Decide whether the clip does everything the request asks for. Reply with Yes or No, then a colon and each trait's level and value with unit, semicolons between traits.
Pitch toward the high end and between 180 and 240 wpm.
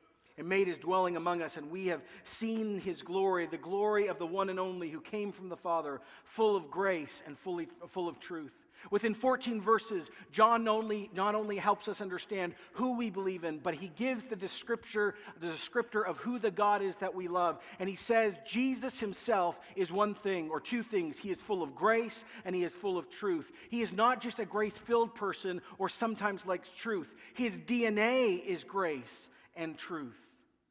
Yes: high, 200 Hz; average, 195 wpm